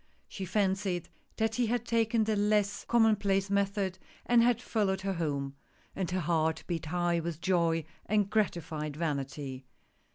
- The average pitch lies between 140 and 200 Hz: Yes, high, 190 Hz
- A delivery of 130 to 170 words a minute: Yes, average, 155 wpm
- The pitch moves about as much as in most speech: Yes, average, 4.3 semitones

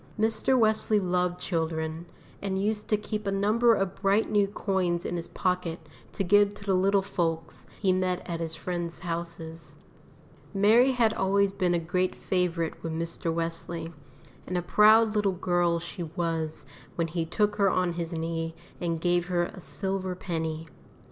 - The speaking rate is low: No, average, 170 wpm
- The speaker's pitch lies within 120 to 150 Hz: No, medium, 180 Hz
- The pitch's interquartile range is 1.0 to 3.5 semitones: Yes, average, 3.1 semitones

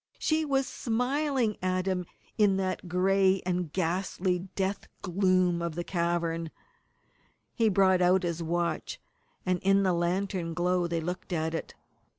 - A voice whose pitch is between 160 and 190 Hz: Yes, medium, 185 Hz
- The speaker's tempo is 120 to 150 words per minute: Yes, average, 145 wpm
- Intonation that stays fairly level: Yes, narrow, 2.1 semitones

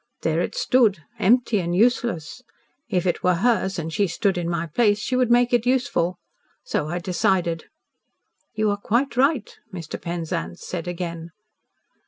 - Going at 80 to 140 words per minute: No, average, 160 wpm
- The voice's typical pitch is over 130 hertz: Yes, high, 190 Hz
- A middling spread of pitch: No, wide, 5.9 semitones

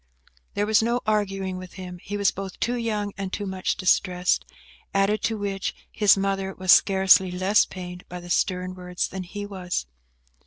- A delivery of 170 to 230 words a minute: Yes, average, 185 wpm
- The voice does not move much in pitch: Yes, narrow, 1.9 semitones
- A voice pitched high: Yes, high, 195 Hz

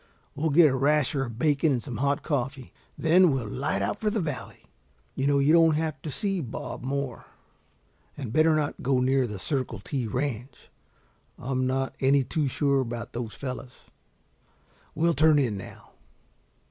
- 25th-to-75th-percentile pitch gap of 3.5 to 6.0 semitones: No, average, 3.1 semitones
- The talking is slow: No, average, 170 wpm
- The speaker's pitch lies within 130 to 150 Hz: Yes, medium, 140 Hz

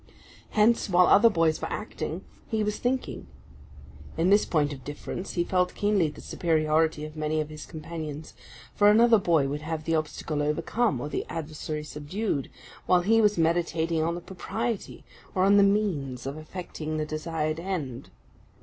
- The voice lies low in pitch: No, medium, 165 Hz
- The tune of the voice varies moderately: Yes, average, 4.4 semitones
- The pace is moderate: Yes, average, 170 wpm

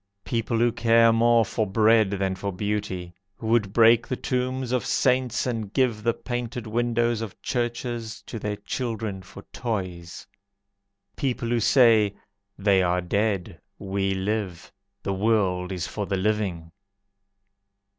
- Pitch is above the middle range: No, low, 110 Hz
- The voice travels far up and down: No, average, 3.4 semitones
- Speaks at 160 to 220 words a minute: No, average, 140 wpm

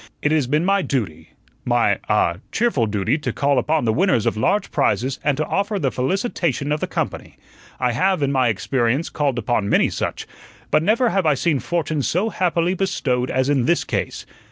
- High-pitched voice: No, medium, 145 Hz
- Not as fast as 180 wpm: No, average, 195 wpm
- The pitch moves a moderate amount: No, wide, 6.0 semitones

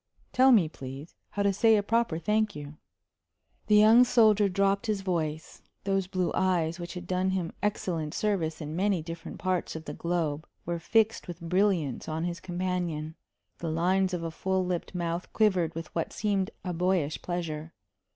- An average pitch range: Yes, average, 3.2 semitones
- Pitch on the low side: No, medium, 180 Hz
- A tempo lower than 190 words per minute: Yes, average, 175 wpm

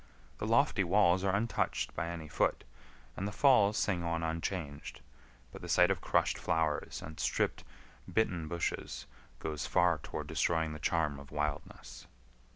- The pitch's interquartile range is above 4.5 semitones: No, average, 3.5 semitones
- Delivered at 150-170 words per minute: Yes, average, 155 wpm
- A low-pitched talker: Yes, very low, 85 Hz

